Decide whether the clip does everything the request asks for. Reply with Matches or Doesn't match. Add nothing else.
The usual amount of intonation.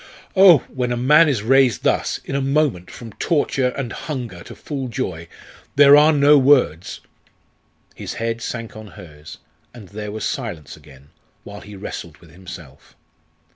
Doesn't match